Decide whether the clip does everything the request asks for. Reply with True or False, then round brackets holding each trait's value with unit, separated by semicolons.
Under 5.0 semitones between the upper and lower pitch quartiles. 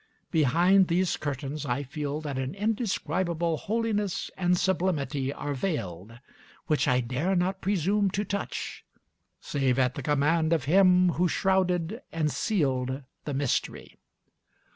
False (5.3 semitones)